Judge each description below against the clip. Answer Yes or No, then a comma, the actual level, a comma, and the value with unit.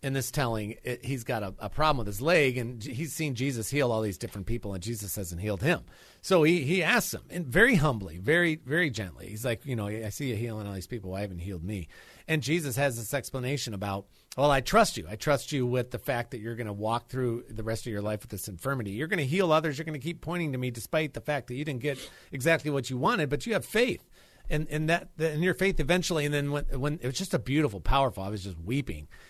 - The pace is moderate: No, fast, 270 wpm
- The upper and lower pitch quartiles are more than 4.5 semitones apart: Yes, wide, 5.6 semitones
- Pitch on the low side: Yes, low, 130 Hz